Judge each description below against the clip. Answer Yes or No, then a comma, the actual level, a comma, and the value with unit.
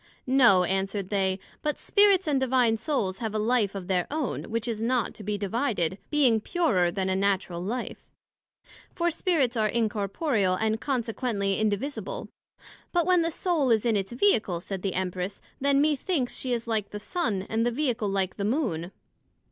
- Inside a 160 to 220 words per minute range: Yes, average, 175 wpm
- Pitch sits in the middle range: No, high, 225 Hz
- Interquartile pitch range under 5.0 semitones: No, wide, 5.6 semitones